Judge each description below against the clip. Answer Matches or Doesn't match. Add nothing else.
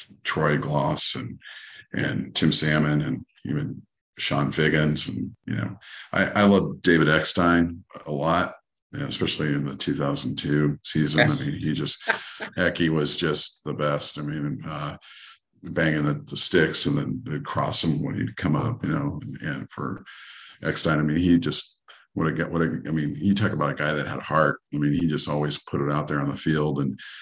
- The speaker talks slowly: Doesn't match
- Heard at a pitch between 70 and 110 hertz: Matches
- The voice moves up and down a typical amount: Doesn't match